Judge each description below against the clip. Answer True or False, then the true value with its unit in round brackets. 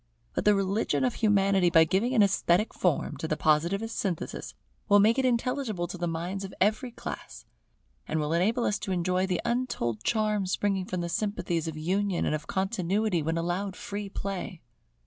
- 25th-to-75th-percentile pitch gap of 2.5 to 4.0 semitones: True (3.6 semitones)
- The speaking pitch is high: True (195 Hz)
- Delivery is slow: False (180 wpm)